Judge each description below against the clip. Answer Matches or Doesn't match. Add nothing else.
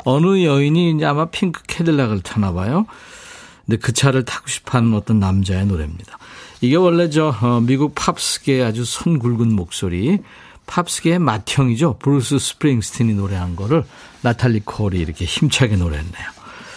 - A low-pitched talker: Matches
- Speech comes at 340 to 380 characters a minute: Matches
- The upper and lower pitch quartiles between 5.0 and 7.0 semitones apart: Doesn't match